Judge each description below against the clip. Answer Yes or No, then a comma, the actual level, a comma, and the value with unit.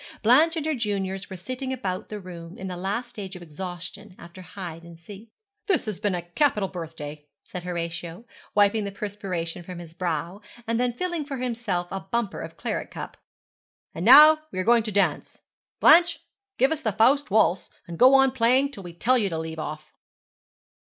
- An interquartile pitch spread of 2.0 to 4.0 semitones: No, wide, 5.6 semitones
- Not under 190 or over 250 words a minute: Yes, average, 195 wpm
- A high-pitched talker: Yes, high, 195 Hz